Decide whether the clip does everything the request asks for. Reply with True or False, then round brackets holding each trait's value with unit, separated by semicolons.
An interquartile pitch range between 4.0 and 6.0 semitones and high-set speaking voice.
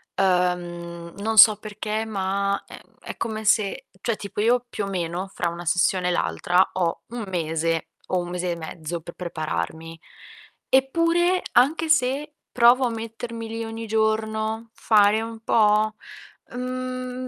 True (4.6 semitones; 215 Hz)